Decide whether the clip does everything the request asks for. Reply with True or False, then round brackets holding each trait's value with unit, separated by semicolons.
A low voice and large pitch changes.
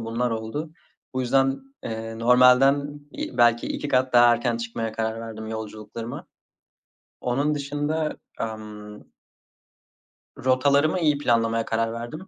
False (120 Hz; 3.6 semitones)